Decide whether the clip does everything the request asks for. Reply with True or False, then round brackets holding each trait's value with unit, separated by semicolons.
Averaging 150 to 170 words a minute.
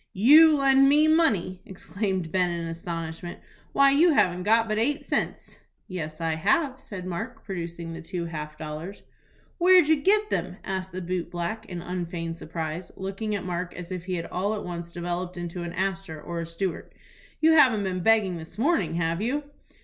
False (185 wpm)